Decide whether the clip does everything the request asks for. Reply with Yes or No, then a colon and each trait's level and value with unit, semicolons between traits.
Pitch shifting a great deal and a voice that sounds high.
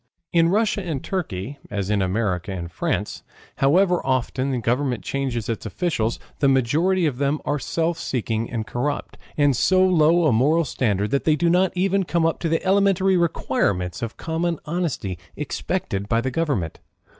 No: wide, 6.8 semitones; medium, 140 Hz